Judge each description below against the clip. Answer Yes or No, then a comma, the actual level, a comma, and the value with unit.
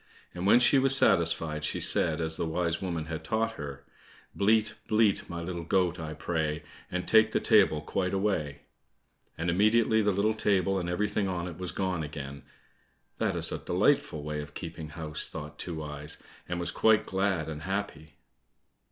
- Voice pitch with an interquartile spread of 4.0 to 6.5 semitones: Yes, average, 4.4 semitones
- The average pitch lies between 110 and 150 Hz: No, very low, 85 Hz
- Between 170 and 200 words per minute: Yes, average, 180 wpm